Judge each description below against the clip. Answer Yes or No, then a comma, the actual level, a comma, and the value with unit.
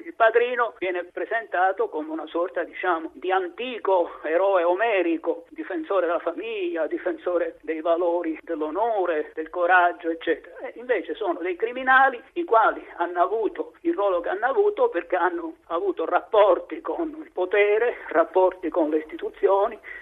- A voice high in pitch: Yes, high, 195 Hz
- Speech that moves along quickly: No, average, 140 wpm